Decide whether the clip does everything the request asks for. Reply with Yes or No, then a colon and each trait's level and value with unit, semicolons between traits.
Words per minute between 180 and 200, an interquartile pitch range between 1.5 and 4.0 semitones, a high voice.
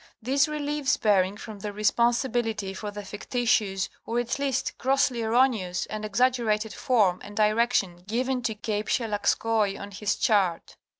No: average, 140 wpm; average, 3.1 semitones; high, 220 Hz